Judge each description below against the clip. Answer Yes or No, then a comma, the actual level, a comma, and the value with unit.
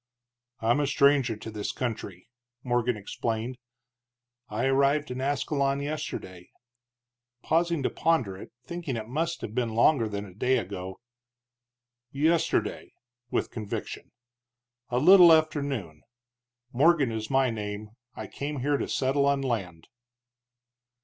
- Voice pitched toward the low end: Yes, low, 125 Hz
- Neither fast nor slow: No, slow, 130 wpm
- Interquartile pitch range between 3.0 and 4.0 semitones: No, average, 4.5 semitones